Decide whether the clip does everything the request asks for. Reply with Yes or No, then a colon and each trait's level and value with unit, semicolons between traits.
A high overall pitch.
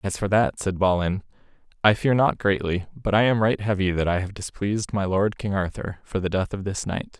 No: low, 100 Hz